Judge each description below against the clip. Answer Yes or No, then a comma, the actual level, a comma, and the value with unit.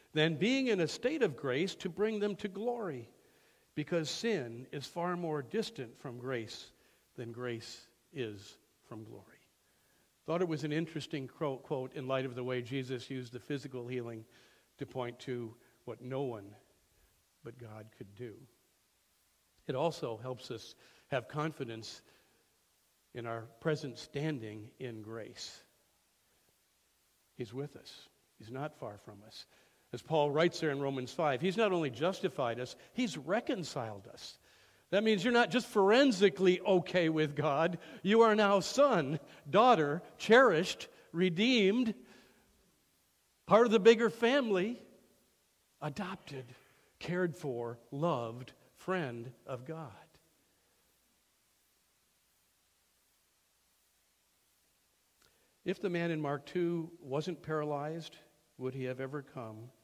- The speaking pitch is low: No, medium, 145 Hz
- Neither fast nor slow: No, slow, 125 wpm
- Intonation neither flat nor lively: No, wide, 6.4 semitones